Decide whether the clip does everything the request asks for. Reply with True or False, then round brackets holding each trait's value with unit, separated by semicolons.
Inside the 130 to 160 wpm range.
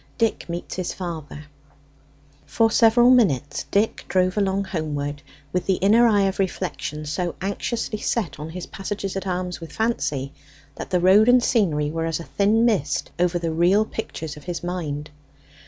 False (170 wpm)